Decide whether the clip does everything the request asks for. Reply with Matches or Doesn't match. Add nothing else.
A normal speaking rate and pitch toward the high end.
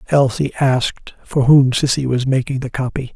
Doesn't match